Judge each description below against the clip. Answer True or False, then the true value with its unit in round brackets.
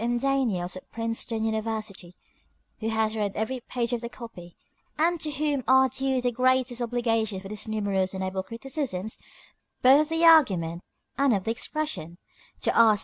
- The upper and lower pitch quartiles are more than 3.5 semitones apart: True (4.3 semitones)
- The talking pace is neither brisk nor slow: True (170 wpm)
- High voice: True (230 Hz)